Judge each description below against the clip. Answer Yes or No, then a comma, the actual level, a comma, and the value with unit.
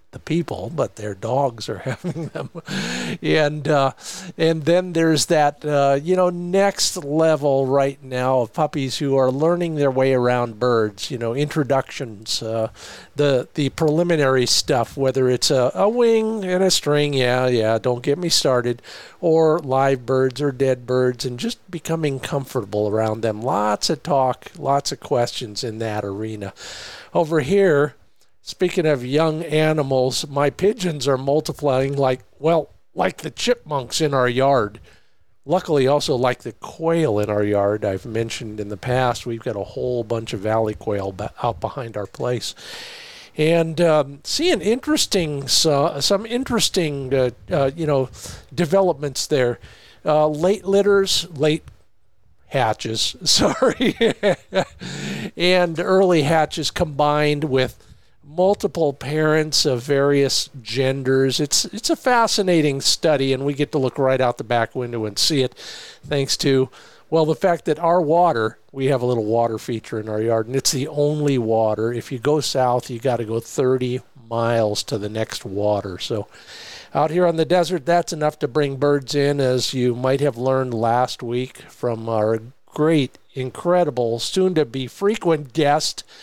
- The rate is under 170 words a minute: Yes, average, 160 wpm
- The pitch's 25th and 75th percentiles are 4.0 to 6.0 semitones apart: Yes, average, 4.7 semitones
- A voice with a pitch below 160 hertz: Yes, medium, 140 Hz